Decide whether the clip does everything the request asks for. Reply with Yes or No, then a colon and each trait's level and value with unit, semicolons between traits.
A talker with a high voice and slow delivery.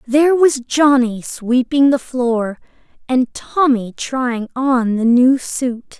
Yes: very high, 255 Hz; slow, 130 wpm